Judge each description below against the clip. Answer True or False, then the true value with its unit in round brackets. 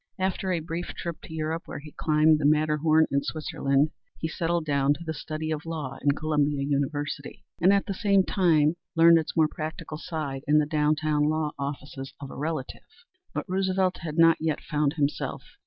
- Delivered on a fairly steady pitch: True (2.0 semitones)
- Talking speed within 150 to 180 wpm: False (190 wpm)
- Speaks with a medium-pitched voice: True (155 Hz)